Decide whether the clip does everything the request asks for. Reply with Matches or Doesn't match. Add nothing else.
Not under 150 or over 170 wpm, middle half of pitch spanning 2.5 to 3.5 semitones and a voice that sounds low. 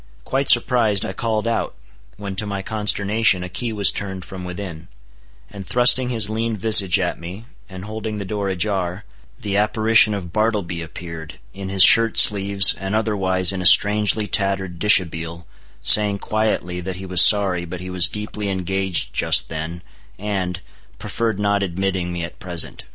Matches